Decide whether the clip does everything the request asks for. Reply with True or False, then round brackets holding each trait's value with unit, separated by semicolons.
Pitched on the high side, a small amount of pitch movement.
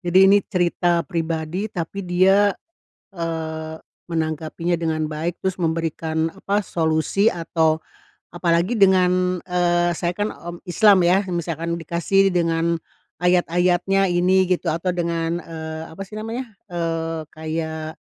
False (170 Hz; 2.0 semitones)